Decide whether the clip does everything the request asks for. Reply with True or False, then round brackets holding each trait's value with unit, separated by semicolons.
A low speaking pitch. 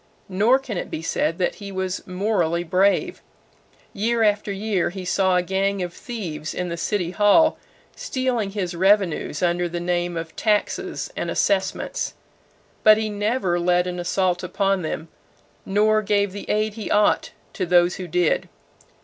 False (190 Hz)